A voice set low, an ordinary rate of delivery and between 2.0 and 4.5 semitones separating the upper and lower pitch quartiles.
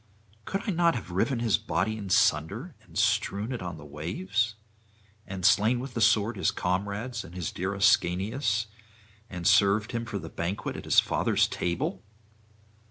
Yes: low, 100 Hz; average, 165 wpm; average, 4.2 semitones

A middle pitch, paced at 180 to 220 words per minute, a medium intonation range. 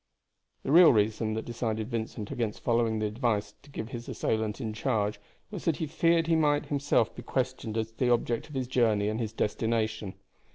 No: low, 115 Hz; average, 200 wpm; average, 3.2 semitones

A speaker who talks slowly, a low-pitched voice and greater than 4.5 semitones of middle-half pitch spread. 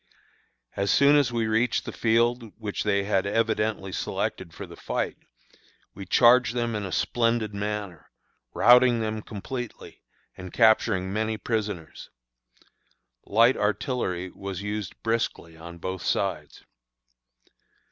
No: slow, 125 wpm; low, 110 Hz; average, 2.9 semitones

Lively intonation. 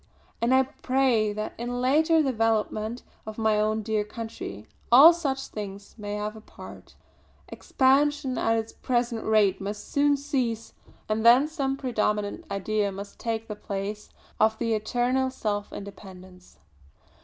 No: average, 3.7 semitones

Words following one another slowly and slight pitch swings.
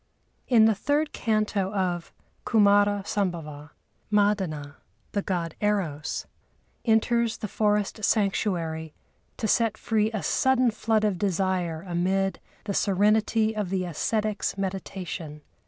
No: slow, 115 wpm; average, 3.2 semitones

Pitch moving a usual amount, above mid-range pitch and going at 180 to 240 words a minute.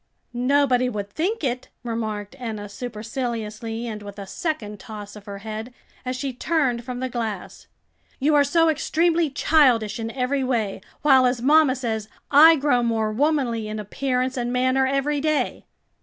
No: average, 4.1 semitones; very high, 250 Hz; average, 160 wpm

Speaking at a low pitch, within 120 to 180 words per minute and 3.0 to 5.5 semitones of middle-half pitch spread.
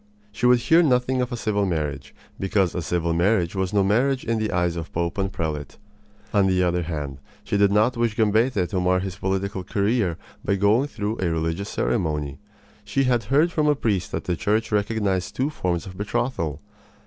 No: low, 100 Hz; average, 195 wpm; average, 4.6 semitones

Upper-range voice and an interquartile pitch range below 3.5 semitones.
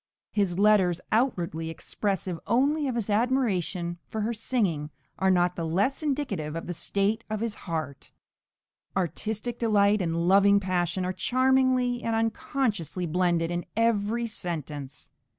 No: high, 200 Hz; average, 4.9 semitones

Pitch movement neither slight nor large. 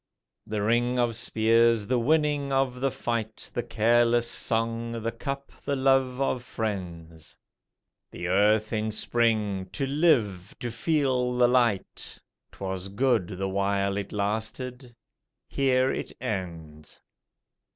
Yes: average, 3.9 semitones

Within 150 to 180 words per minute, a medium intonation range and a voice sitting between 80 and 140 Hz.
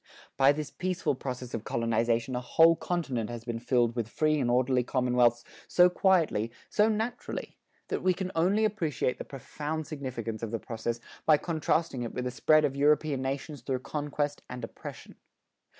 Yes: average, 170 wpm; average, 4.7 semitones; low, 135 Hz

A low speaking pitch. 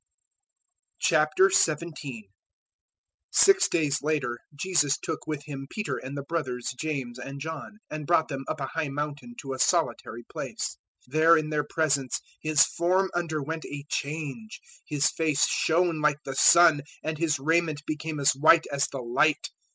No: medium, 155 Hz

